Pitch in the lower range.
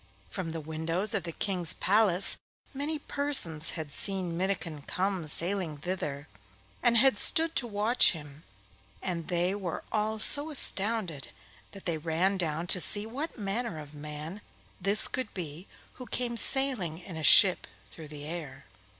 No: medium, 185 Hz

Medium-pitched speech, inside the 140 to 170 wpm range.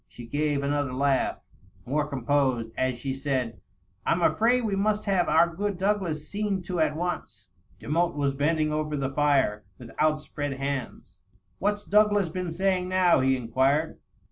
Yes: medium, 150 Hz; average, 160 wpm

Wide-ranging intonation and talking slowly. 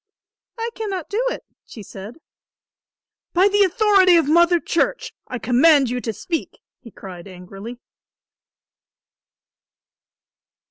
Yes: wide, 9.0 semitones; slow, 110 wpm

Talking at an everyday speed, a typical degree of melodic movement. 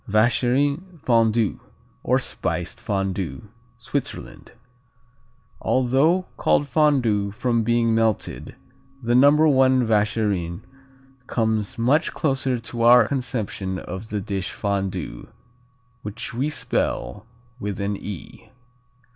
No: slow, 100 wpm; average, 4.4 semitones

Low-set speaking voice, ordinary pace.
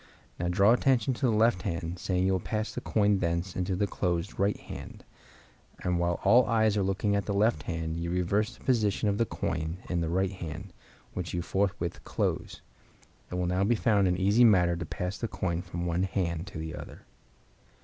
No: very low, 95 Hz; fast, 210 wpm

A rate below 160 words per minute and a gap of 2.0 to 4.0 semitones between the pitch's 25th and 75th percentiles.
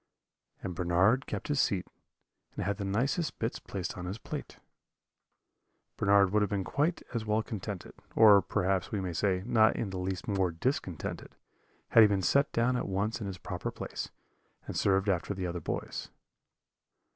No: average, 175 wpm; average, 3.2 semitones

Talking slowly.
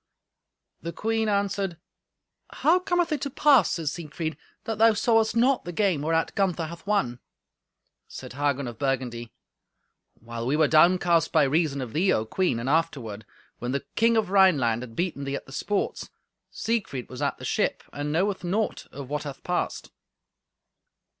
No: average, 165 wpm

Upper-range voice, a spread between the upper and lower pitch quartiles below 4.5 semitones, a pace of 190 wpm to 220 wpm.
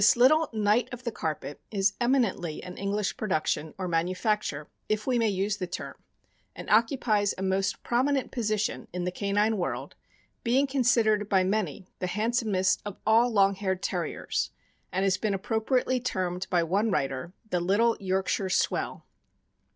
No: high, 205 Hz; average, 3.6 semitones; average, 160 wpm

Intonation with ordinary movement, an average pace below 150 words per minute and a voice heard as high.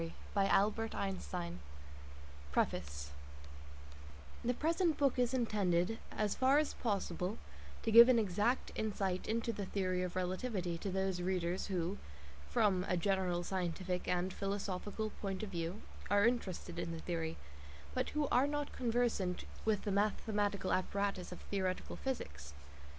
Yes: average, 3.7 semitones; slow, 135 wpm; high, 195 Hz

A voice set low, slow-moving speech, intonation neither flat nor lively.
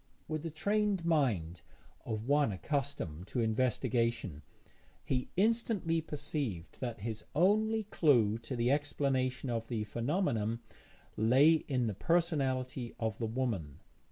No: low, 130 Hz; slow, 125 wpm; wide, 5.7 semitones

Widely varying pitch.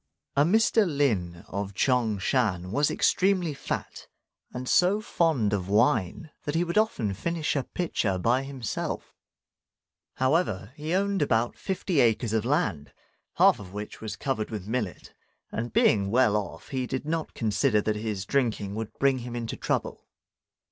Yes: wide, 6.2 semitones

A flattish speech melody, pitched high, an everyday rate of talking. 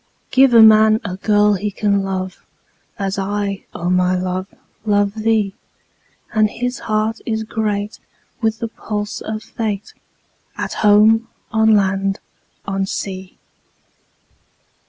No: narrow, 2.0 semitones; high, 210 Hz; slow, 130 wpm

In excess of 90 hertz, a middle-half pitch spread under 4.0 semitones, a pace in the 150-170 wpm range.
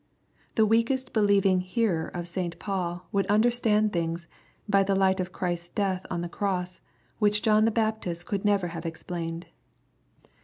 Yes: high, 190 Hz; average, 3.4 semitones; average, 160 wpm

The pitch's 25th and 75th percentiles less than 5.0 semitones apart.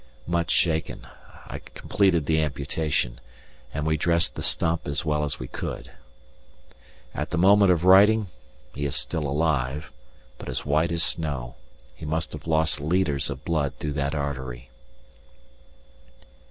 Yes: average, 2.9 semitones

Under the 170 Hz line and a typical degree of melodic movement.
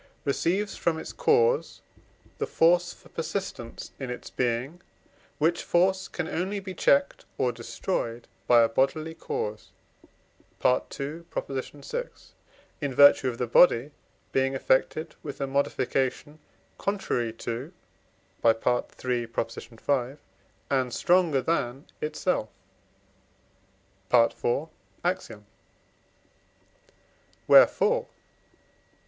No: medium, 140 Hz; wide, 5.9 semitones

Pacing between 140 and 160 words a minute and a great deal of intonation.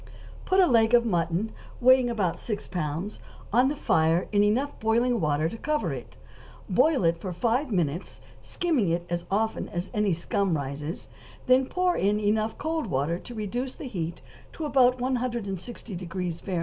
No: average, 175 wpm; wide, 6.3 semitones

